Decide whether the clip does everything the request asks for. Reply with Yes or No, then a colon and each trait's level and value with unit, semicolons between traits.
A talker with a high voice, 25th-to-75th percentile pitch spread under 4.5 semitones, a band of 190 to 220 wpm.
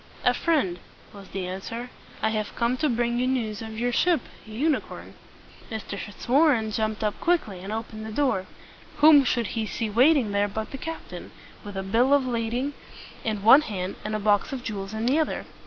Yes: high, 225 Hz; average, 3.9 semitones; average, 200 wpm